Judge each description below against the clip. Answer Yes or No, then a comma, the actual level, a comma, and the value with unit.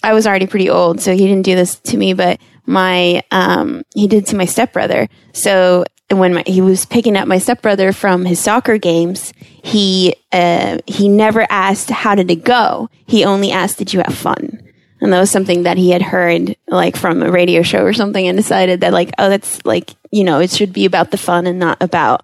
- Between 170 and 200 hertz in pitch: Yes, high, 190 Hz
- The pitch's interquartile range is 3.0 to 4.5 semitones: No, narrow, 2.6 semitones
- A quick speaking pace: Yes, fast, 225 wpm